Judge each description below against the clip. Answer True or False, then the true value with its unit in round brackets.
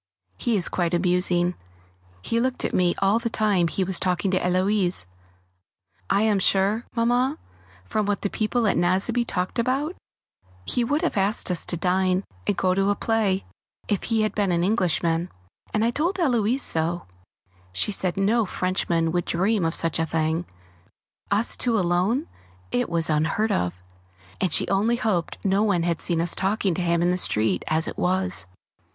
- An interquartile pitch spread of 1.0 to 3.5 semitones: False (4.0 semitones)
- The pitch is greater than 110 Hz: True (190 Hz)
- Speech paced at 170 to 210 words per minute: True (180 wpm)